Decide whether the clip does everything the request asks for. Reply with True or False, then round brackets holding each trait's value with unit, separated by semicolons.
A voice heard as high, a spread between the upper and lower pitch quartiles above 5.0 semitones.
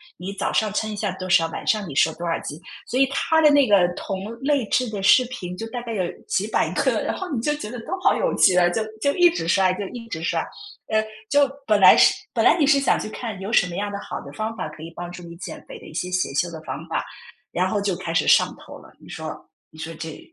True (200 Hz; 5.4 semitones)